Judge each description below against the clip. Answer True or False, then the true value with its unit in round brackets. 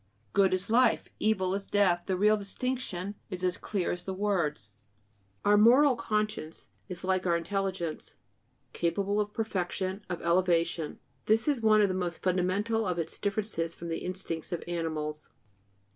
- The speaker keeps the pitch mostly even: False (3.2 semitones)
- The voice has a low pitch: False (185 Hz)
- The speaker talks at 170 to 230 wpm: False (160 wpm)